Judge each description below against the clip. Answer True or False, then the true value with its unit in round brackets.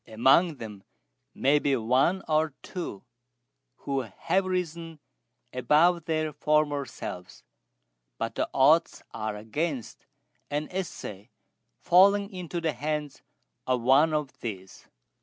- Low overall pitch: False (150 Hz)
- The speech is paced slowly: True (115 wpm)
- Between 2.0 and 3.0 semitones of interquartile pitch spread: False (4.8 semitones)